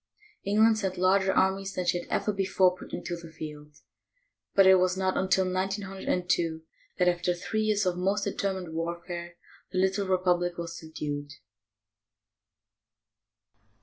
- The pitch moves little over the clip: Yes, narrow, 1.9 semitones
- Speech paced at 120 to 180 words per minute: Yes, average, 140 wpm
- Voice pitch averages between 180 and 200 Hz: Yes, medium, 185 Hz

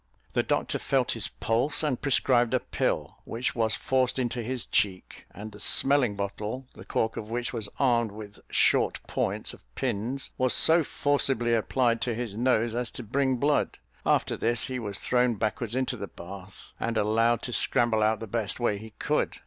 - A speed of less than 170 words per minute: No, average, 185 wpm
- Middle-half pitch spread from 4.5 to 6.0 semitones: No, average, 2.8 semitones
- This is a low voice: Yes, low, 115 Hz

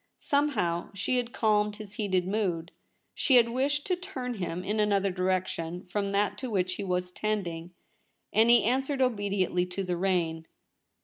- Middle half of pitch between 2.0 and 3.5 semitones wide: No, average, 4.5 semitones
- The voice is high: Yes, high, 200 Hz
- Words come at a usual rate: Yes, average, 165 wpm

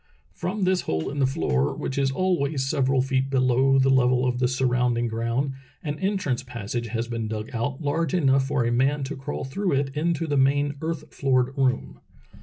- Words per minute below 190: No, average, 195 wpm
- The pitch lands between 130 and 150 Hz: Yes, low, 135 Hz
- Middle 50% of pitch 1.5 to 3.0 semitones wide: Yes, average, 2.7 semitones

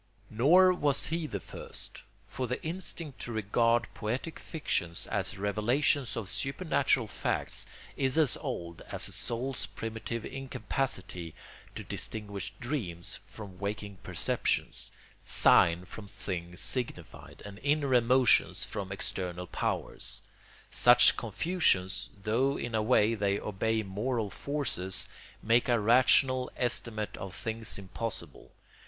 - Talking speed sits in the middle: No, slow, 120 wpm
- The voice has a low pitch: Yes, low, 115 Hz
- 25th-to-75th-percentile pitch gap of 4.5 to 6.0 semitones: Yes, average, 4.8 semitones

